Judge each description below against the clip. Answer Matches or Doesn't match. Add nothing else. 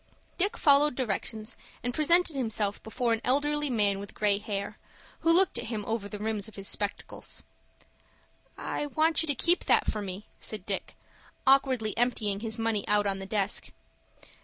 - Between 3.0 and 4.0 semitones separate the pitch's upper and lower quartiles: Doesn't match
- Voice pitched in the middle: Doesn't match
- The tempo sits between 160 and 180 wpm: Matches